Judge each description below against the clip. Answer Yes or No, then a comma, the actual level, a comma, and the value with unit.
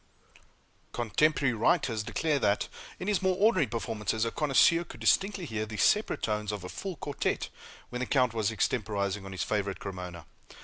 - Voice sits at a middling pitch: No, low, 115 Hz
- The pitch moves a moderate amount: No, wide, 6.6 semitones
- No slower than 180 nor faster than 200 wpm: No, average, 170 wpm